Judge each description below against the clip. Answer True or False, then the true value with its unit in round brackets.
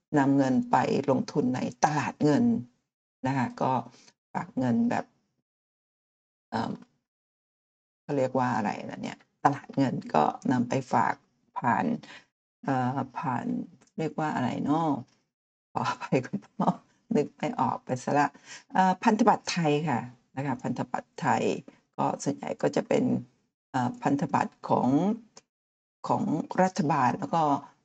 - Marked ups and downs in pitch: True (6.7 semitones)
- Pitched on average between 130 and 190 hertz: True (140 Hz)